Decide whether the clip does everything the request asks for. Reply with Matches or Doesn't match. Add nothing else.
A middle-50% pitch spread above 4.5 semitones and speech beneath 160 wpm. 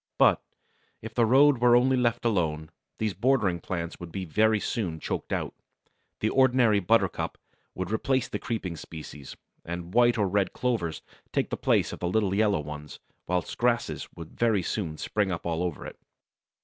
Doesn't match